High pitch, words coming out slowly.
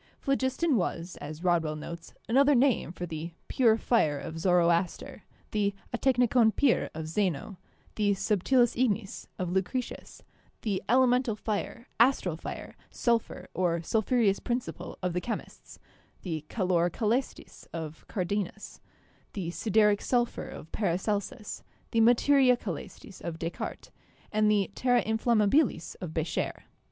Yes: high, 205 Hz; slow, 125 wpm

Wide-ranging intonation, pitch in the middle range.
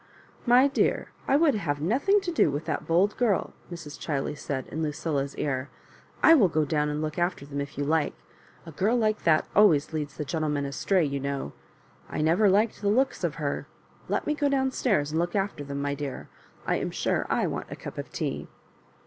Yes: wide, 6.6 semitones; medium, 160 Hz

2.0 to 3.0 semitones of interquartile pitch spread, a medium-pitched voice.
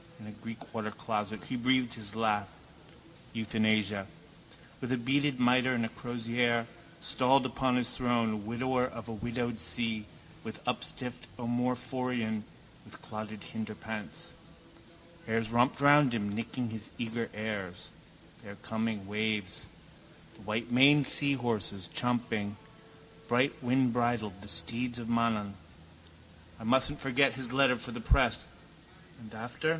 No: narrow, 2.5 semitones; low, 115 Hz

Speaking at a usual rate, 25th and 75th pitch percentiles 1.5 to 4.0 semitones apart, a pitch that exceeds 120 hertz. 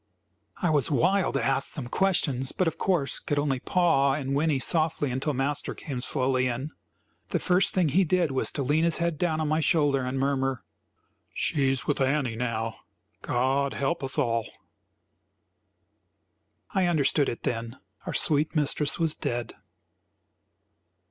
Yes: average, 155 wpm; average, 3.4 semitones; medium, 140 Hz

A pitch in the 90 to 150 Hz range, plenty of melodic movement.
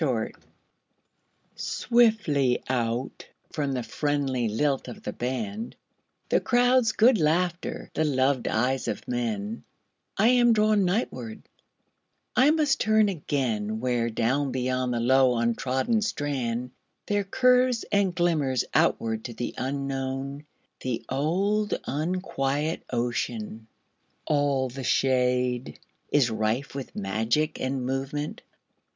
Yes: low, 135 Hz; wide, 6.6 semitones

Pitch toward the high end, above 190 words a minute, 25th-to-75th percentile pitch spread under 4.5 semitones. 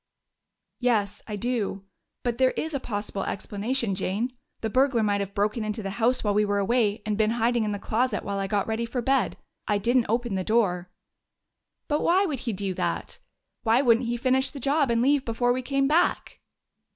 Yes: high, 230 Hz; average, 200 wpm; average, 3.7 semitones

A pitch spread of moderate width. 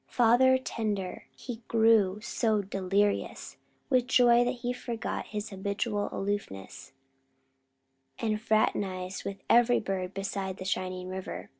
Yes: average, 3.6 semitones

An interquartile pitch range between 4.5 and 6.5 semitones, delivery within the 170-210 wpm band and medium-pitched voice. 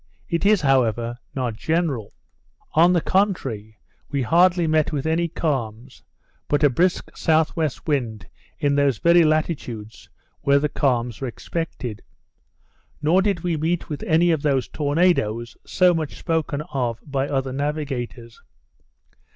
No: average, 5.1 semitones; slow, 135 wpm; medium, 145 Hz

